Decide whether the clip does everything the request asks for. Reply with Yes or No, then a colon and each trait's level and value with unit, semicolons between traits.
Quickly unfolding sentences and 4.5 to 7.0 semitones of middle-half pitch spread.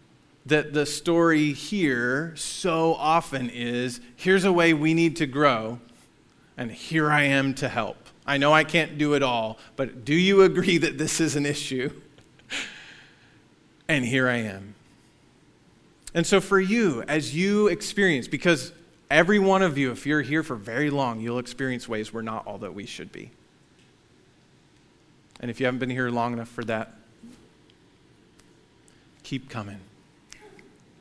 No: average, 155 wpm; average, 5.0 semitones